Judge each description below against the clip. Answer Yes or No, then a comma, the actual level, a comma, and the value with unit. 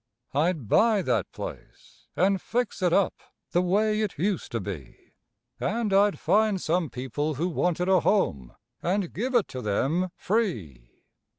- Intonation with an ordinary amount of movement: No, wide, 7.0 semitones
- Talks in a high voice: No, medium, 180 Hz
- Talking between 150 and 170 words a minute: Yes, average, 155 wpm